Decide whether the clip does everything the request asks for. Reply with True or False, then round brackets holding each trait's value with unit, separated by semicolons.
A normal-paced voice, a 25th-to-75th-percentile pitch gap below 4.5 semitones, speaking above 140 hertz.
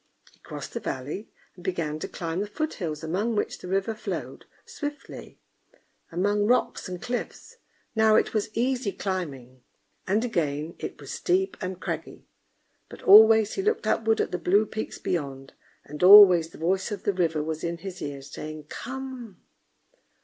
False (165 wpm; 5.2 semitones; 190 Hz)